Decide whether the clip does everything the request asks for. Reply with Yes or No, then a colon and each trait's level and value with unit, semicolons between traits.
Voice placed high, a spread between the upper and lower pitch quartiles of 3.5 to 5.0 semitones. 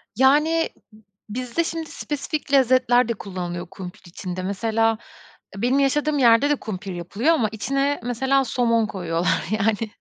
No: high, 235 Hz; wide, 5.4 semitones